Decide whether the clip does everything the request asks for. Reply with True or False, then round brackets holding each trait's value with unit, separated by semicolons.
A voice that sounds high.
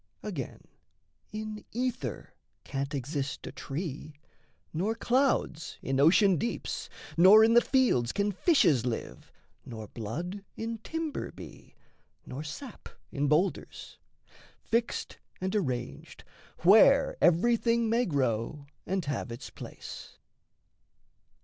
False (180 Hz)